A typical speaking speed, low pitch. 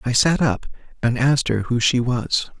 No: fast, 210 wpm; low, 125 Hz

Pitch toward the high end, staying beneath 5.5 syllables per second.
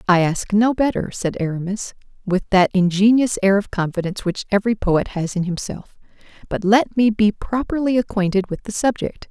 Yes: high, 205 Hz; 5.3 syllables/s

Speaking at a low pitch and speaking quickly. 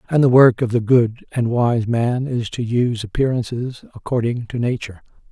No: low, 120 Hz; average, 180 wpm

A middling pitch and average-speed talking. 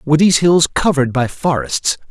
Yes: medium, 150 Hz; average, 170 wpm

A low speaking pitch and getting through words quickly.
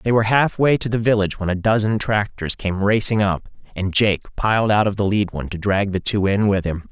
Yes: low, 100 Hz; fast, 245 wpm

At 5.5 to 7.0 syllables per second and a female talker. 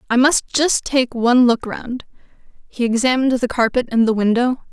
No: 5.2 syllables/s; female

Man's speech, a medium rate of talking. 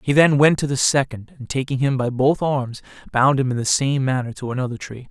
No: male; fast, 245 wpm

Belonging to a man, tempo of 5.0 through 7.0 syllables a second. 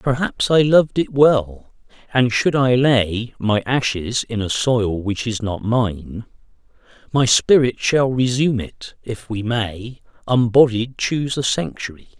No: male; 3.9 syllables/s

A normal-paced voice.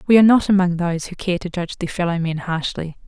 No: fast, 255 wpm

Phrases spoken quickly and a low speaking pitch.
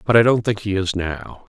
Yes: fast, 270 wpm; low, 100 Hz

